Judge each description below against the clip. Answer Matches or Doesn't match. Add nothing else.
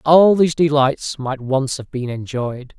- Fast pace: Doesn't match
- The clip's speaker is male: Matches